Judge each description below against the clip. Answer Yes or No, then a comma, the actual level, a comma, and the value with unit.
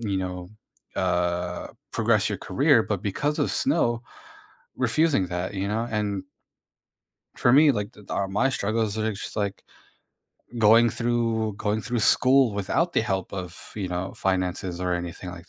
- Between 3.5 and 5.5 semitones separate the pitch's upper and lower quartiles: Yes, average, 4.2 semitones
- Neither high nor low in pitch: No, low, 105 Hz